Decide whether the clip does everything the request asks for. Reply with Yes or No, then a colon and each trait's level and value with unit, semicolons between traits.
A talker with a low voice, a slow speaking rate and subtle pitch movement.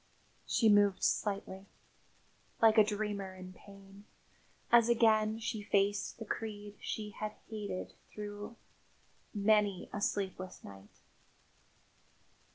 No: high, 205 Hz; slow, 105 wpm; narrow, 1.6 semitones